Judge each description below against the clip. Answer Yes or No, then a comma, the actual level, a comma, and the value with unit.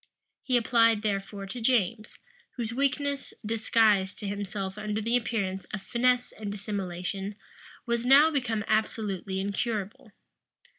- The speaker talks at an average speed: No, slow, 120 wpm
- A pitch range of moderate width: Yes, average, 3.1 semitones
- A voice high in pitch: Yes, high, 215 Hz